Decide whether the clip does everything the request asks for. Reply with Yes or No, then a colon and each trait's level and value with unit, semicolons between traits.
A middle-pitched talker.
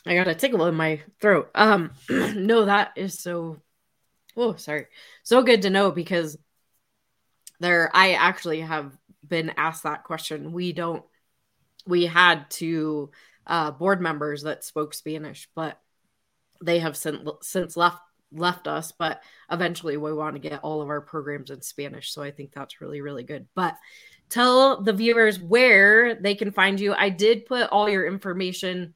Yes: medium, 170 Hz